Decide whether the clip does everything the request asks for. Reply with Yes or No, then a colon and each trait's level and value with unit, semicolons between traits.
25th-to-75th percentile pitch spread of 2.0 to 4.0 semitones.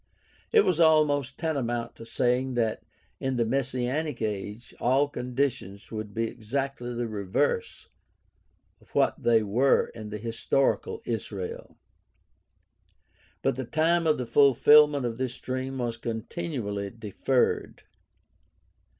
Yes: average, 3.4 semitones